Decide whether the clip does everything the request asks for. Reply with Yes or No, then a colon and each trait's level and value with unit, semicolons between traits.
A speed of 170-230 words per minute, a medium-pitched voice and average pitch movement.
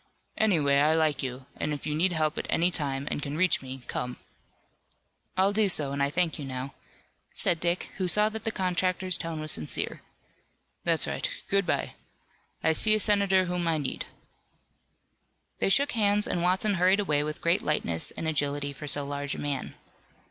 Yes: average, 185 wpm; medium, 160 Hz; average, 4.7 semitones